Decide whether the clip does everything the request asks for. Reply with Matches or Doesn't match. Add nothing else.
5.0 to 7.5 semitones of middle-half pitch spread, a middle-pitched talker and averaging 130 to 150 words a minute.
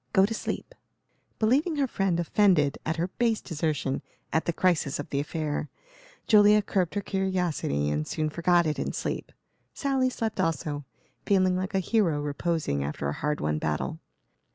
Doesn't match